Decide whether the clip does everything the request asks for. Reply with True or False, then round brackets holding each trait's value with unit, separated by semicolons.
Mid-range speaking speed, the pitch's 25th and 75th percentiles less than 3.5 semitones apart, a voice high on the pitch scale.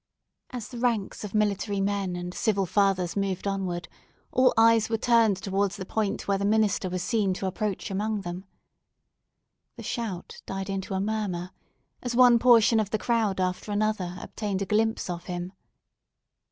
True (165 wpm; 2.6 semitones; 200 Hz)